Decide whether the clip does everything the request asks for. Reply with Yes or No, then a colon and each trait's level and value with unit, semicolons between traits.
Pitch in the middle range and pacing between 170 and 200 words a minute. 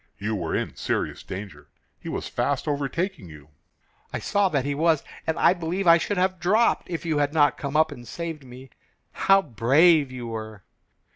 Yes: medium, 145 Hz; average, 190 wpm